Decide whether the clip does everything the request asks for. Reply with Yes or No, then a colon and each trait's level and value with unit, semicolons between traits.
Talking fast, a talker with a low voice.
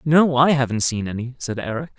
Yes: fast, 210 wpm; low, 130 Hz